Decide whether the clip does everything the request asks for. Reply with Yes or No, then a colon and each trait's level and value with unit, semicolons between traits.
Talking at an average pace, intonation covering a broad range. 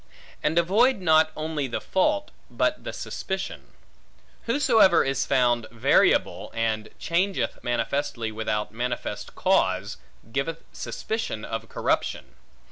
No: slow, 110 wpm; wide, 8.4 semitones